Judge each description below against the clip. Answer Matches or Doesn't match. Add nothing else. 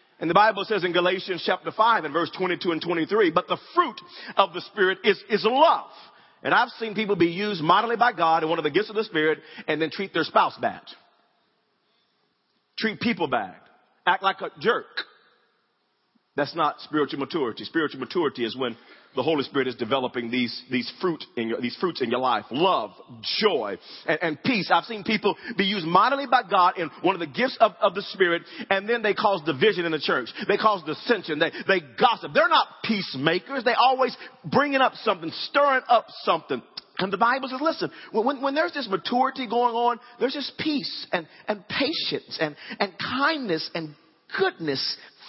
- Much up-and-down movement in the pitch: Matches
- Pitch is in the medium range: Doesn't match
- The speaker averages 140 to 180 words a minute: Doesn't match